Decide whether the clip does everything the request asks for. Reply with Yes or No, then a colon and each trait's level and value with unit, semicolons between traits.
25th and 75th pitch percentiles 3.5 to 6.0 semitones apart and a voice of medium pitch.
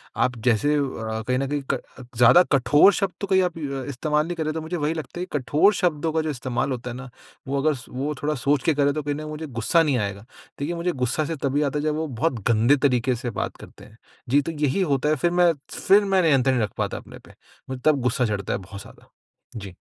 Yes: average, 4.0 semitones; medium, 145 Hz